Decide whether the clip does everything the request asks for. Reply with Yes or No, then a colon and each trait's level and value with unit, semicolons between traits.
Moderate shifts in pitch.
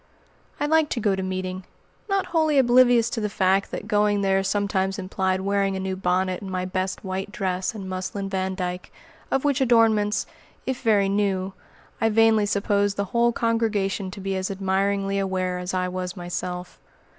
No: narrow, 2.3 semitones